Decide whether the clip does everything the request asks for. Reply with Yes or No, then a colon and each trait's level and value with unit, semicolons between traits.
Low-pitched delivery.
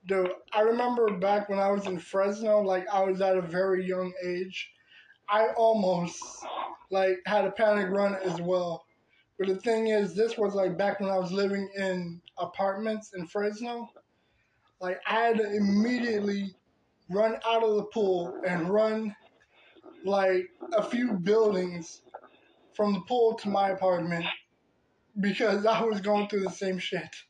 No: high, 200 Hz